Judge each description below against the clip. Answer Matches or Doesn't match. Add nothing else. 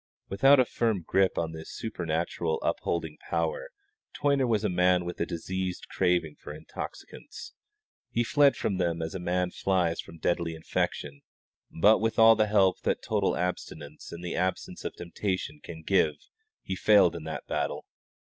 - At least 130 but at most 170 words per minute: Matches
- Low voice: Matches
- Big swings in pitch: Doesn't match